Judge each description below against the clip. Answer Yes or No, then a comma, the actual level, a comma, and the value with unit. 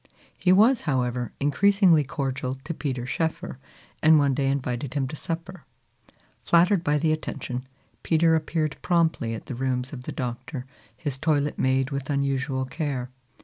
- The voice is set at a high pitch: No, medium, 140 Hz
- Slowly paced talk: No, average, 150 wpm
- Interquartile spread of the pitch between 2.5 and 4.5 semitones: Yes, average, 3.7 semitones